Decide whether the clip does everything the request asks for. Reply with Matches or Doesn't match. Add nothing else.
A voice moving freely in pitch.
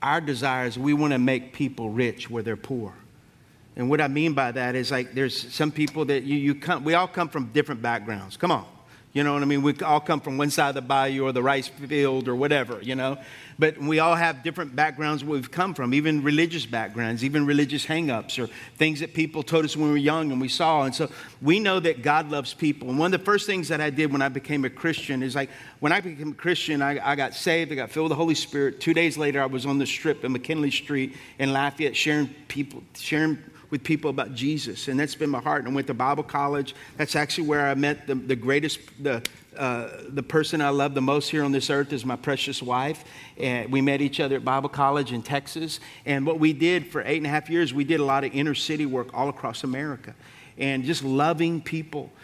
Doesn't match